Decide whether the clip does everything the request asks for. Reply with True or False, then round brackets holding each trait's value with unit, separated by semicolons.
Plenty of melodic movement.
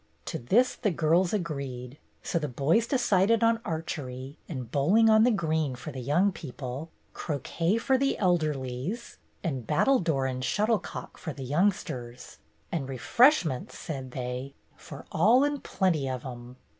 True (7.6 semitones)